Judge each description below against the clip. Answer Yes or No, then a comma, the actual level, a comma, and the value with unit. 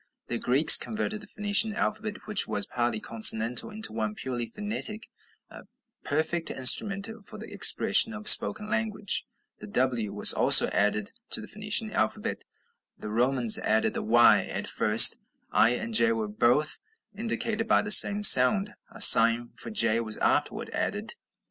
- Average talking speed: Yes, average, 155 wpm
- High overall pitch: No, medium, 155 Hz